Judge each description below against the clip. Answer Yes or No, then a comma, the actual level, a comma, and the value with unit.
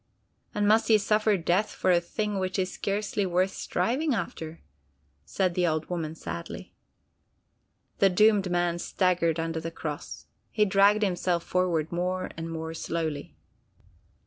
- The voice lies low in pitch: No, medium, 180 Hz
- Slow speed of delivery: No, average, 145 wpm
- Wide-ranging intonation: No, average, 3.4 semitones